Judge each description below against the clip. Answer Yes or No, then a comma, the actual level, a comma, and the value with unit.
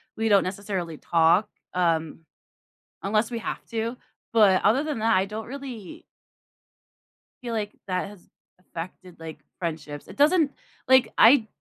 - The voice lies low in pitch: No, high, 205 Hz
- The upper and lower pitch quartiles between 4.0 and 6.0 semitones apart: Yes, average, 4.6 semitones